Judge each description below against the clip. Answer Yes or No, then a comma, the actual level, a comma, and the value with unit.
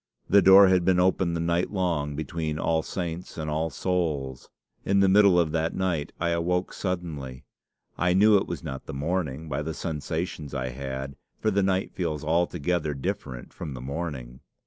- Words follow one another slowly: No, average, 180 wpm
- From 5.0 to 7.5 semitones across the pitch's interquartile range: No, average, 3.7 semitones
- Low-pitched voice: Yes, very low, 85 Hz